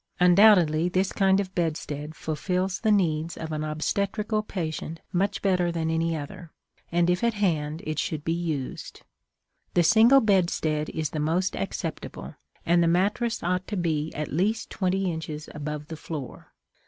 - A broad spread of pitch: No, average, 3.6 semitones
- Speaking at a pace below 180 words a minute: Yes, average, 160 wpm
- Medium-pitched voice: Yes, medium, 170 Hz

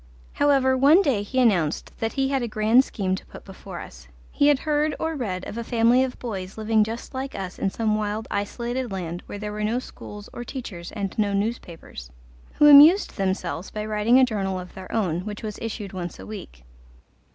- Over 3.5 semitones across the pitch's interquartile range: Yes, average, 4.9 semitones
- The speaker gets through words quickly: Yes, fast, 210 wpm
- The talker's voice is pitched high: Yes, high, 215 Hz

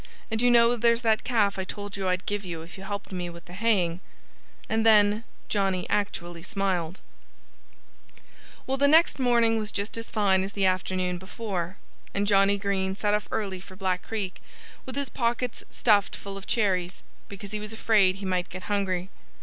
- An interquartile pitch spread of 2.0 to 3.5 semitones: Yes, average, 3.0 semitones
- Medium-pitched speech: No, high, 200 Hz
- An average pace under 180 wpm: No, average, 185 wpm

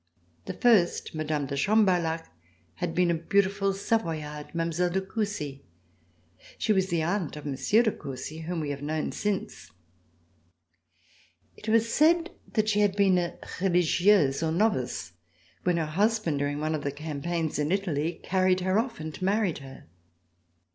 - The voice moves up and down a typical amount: Yes, average, 4.6 semitones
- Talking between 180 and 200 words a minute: No, average, 155 wpm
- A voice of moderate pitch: Yes, medium, 175 Hz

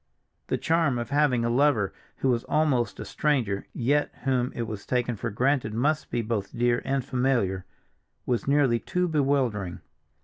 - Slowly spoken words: No, average, 165 wpm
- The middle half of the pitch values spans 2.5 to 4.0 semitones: Yes, average, 3.5 semitones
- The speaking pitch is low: Yes, low, 125 Hz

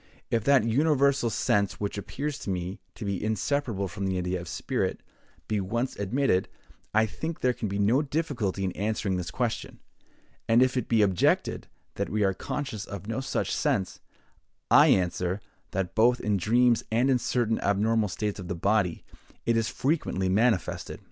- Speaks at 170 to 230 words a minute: Yes, average, 175 wpm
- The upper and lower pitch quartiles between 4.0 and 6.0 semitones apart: Yes, average, 4.3 semitones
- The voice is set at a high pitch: No, low, 110 Hz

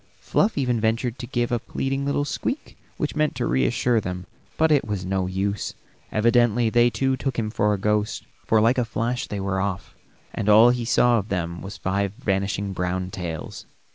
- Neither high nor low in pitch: No, low, 110 Hz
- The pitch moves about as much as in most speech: Yes, average, 4.0 semitones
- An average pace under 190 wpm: No, average, 195 wpm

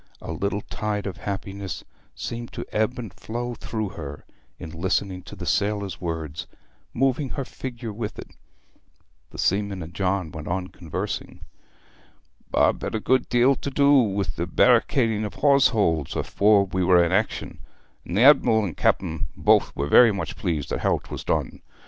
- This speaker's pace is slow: No, average, 165 wpm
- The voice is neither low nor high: No, low, 100 Hz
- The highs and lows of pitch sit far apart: No, average, 4.4 semitones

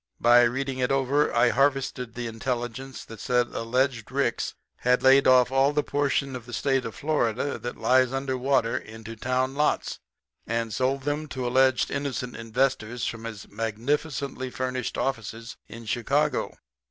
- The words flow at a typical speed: Yes, average, 155 wpm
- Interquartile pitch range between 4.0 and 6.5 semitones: No, average, 2.7 semitones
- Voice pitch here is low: Yes, low, 130 Hz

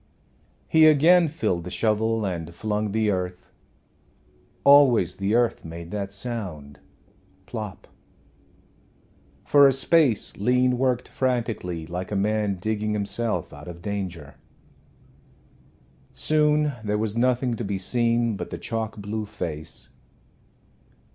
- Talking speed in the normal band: No, slow, 120 wpm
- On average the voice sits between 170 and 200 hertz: No, low, 105 Hz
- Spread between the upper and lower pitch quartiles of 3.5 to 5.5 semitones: Yes, average, 4.7 semitones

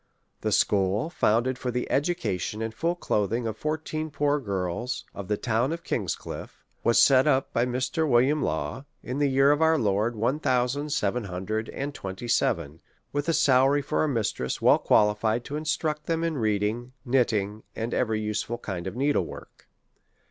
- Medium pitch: No, low, 125 Hz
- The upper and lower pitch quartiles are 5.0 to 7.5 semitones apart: Yes, average, 5.3 semitones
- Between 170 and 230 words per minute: Yes, average, 180 wpm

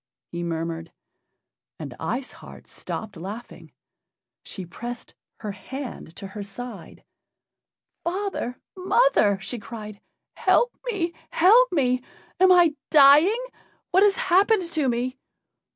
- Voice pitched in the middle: No, very high, 255 Hz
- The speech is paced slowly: Yes, slow, 115 wpm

